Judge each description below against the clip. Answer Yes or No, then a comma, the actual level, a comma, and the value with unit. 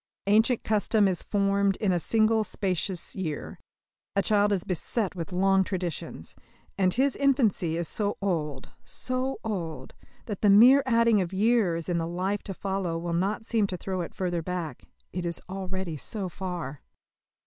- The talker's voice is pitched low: No, high, 190 Hz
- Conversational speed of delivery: Yes, average, 165 wpm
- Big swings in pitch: No, average, 3.3 semitones